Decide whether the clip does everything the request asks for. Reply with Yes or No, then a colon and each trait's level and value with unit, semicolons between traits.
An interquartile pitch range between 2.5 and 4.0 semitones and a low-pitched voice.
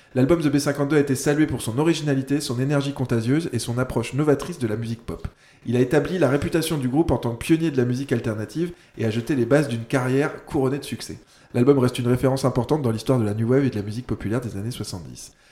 Yes: average, 3.6 semitones; low, 130 Hz